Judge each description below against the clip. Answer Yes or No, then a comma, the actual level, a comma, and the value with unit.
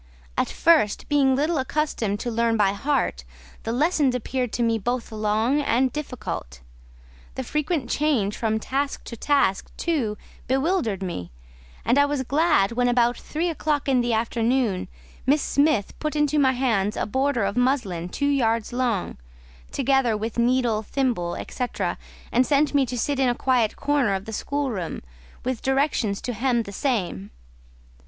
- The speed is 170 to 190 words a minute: No, average, 160 wpm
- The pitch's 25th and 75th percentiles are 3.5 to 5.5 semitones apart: Yes, average, 4.4 semitones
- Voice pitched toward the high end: Yes, very high, 250 Hz